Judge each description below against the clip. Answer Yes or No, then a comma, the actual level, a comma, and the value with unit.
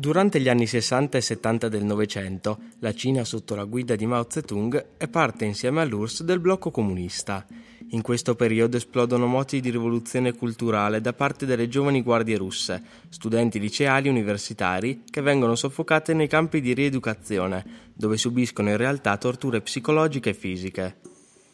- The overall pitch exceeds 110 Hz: Yes, low, 120 Hz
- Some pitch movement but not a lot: Yes, average, 4.2 semitones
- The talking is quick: No, average, 155 wpm